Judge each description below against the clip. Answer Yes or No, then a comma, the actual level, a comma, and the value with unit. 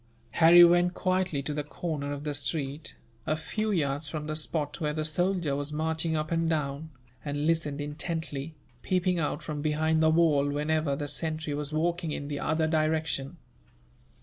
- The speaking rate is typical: Yes, average, 175 wpm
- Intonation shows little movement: Yes, narrow, 2.1 semitones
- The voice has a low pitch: No, medium, 155 Hz